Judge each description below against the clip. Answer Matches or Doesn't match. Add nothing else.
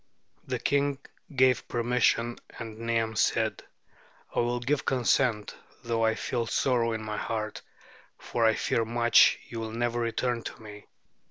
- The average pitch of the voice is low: Matches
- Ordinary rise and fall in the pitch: Doesn't match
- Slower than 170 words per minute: Matches